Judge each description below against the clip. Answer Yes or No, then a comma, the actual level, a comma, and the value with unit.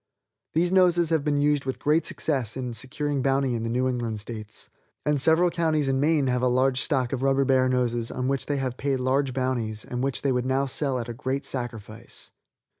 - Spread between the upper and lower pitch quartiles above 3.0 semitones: No, narrow, 2.5 semitones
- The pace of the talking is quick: Yes, fast, 215 wpm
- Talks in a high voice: No, low, 130 Hz